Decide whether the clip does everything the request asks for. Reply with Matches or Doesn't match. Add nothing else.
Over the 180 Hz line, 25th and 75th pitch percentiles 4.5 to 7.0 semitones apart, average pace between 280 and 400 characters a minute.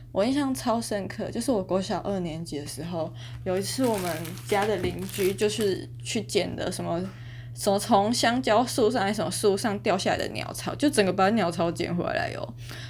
Matches